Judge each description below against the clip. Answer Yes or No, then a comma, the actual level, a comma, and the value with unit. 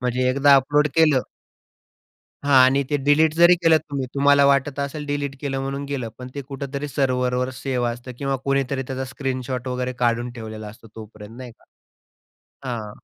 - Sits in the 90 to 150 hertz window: Yes, low, 135 Hz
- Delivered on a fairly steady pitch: Yes, narrow, 2.0 semitones